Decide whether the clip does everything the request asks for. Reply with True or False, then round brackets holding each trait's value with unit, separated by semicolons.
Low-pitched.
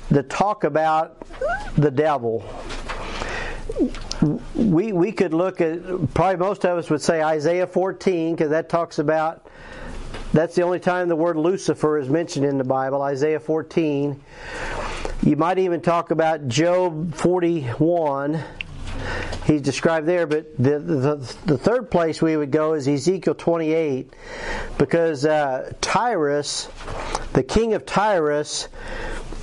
False (160 Hz)